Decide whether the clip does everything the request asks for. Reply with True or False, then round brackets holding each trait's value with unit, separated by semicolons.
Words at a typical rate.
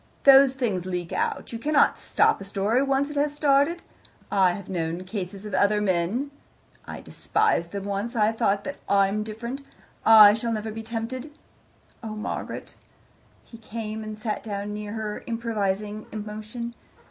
True (160 wpm)